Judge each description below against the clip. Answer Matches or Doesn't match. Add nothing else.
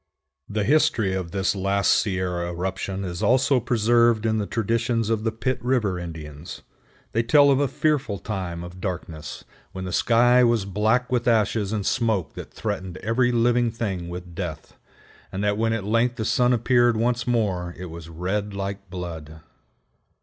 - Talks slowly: Doesn't match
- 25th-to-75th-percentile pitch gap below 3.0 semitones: Doesn't match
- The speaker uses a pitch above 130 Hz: Doesn't match